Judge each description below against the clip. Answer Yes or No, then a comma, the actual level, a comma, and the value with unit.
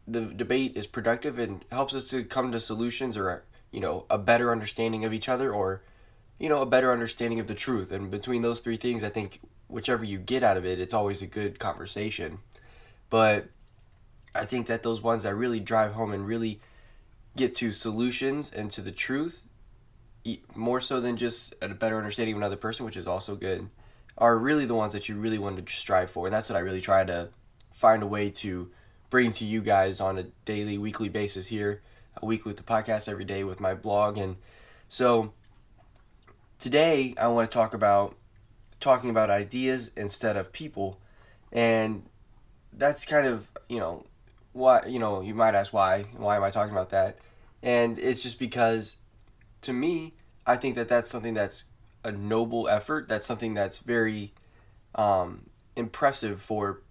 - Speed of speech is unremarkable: Yes, average, 185 wpm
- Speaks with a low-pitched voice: Yes, low, 110 Hz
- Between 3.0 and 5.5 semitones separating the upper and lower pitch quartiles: No, narrow, 2.5 semitones